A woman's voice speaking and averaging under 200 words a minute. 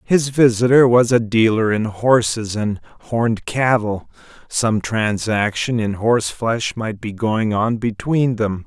No: male; average, 140 wpm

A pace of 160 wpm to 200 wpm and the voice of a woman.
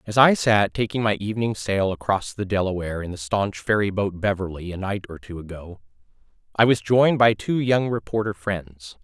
No: average, 195 wpm; male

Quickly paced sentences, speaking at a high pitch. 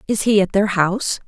Yes: fast, 235 wpm; high, 200 Hz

